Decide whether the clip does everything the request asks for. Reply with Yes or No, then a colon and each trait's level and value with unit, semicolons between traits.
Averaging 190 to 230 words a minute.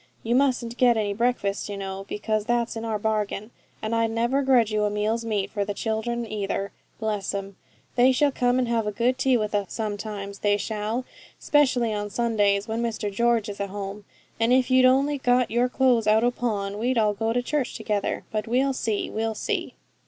Yes: fast, 205 wpm